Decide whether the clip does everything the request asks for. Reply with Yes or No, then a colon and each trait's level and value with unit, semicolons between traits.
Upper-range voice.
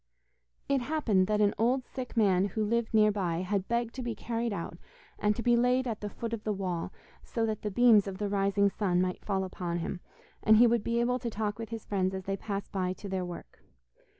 Yes: high, 210 Hz